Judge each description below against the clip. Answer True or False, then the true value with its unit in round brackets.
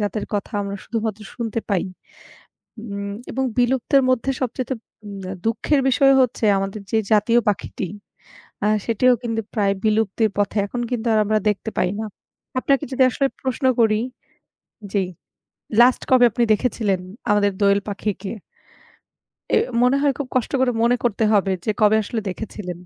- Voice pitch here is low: False (220 Hz)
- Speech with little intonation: False (3.4 semitones)